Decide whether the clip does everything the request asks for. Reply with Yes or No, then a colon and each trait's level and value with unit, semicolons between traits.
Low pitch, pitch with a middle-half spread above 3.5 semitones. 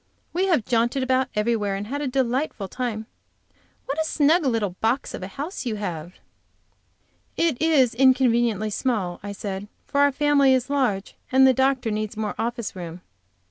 No: high, 240 Hz; average, 4.5 semitones